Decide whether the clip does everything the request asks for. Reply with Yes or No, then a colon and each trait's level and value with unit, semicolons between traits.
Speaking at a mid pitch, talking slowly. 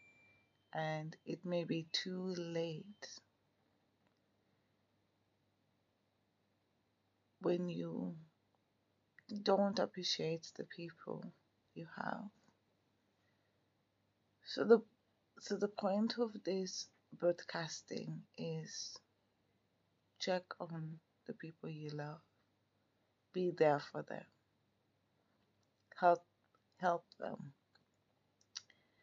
Yes: medium, 145 Hz; slow, 75 wpm